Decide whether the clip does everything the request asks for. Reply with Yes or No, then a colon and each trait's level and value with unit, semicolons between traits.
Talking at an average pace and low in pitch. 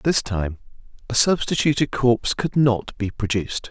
Yes: average, 145 wpm; low, 120 Hz